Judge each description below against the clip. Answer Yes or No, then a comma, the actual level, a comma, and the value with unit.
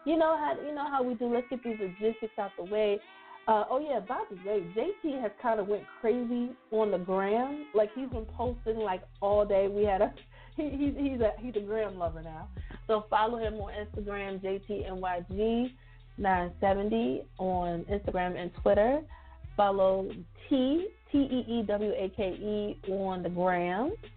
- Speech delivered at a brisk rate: No, average, 190 wpm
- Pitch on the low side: No, high, 210 Hz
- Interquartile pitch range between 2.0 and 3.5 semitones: No, average, 4.0 semitones